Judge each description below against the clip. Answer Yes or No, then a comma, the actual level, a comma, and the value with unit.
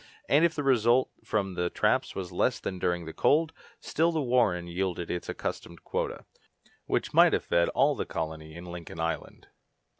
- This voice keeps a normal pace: Yes, average, 180 wpm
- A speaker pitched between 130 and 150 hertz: No, very low, 90 Hz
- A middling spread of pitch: No, wide, 7.1 semitones